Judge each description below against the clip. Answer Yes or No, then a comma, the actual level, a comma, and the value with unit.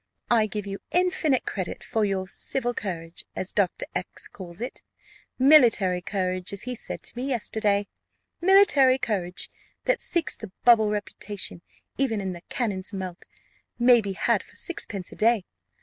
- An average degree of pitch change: Yes, average, 4.8 semitones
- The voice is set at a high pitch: Yes, high, 210 Hz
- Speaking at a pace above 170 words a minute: No, average, 155 wpm